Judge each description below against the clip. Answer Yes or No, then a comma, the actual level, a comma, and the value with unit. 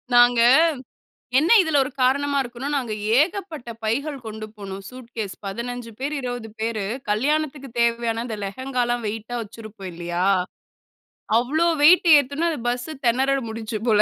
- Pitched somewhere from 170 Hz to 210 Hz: No, high, 240 Hz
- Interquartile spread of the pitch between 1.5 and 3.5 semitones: No, average, 4.0 semitones